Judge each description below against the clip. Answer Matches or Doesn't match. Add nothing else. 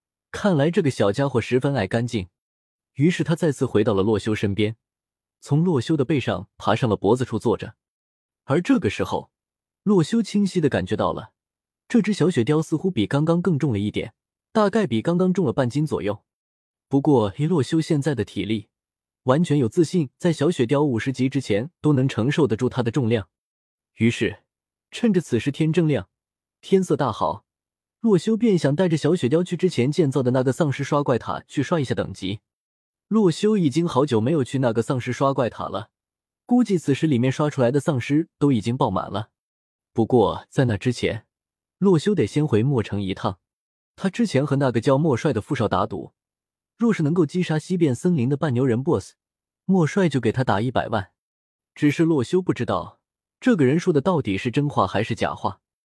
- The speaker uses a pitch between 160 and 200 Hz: Doesn't match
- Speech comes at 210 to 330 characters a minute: Matches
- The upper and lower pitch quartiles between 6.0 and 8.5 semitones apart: Matches